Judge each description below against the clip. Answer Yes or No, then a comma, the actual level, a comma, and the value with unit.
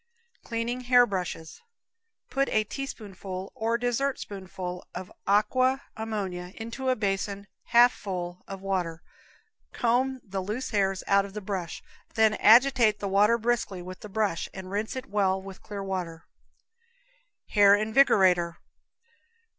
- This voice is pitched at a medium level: No, high, 205 Hz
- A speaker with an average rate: No, slow, 130 wpm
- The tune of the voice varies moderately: Yes, average, 3.5 semitones